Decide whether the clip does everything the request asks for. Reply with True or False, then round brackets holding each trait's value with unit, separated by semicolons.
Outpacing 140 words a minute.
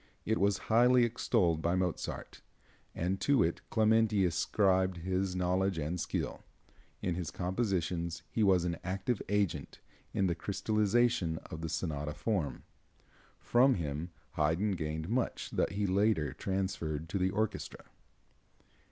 False (135 wpm)